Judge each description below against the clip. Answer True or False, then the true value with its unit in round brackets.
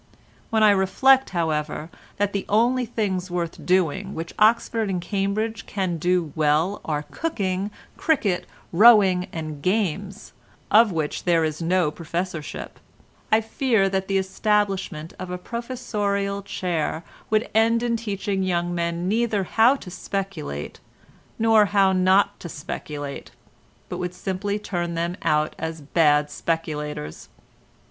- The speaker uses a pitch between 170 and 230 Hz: True (190 Hz)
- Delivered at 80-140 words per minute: True (135 wpm)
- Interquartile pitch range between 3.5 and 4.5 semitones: True (3.9 semitones)